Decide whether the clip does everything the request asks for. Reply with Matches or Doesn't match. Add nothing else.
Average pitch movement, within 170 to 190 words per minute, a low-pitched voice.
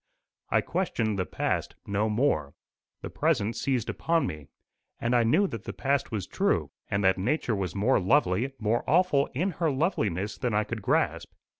Doesn't match